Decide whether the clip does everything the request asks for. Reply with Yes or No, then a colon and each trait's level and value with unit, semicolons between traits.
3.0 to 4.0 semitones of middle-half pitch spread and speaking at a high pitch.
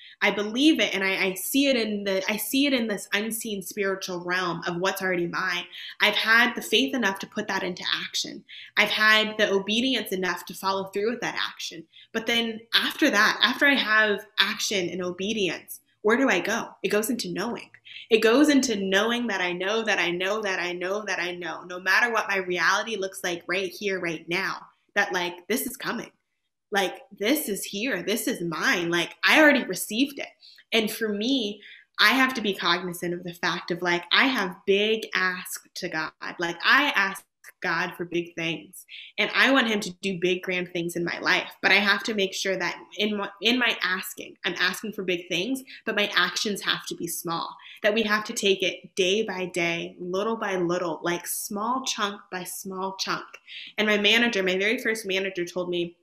Yes: average, 3.3 semitones; high, 195 Hz